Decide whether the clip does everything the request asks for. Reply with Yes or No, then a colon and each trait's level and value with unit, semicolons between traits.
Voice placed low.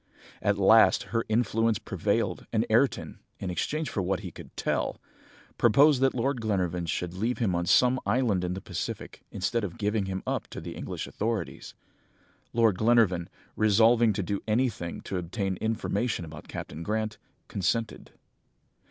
Yes: low, 105 Hz